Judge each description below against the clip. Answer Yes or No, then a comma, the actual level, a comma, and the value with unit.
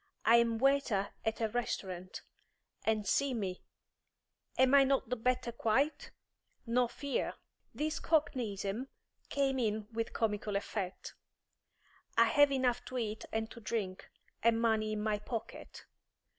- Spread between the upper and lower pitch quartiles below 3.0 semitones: No, average, 3.3 semitones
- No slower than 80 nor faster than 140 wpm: Yes, slow, 135 wpm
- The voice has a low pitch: No, high, 230 Hz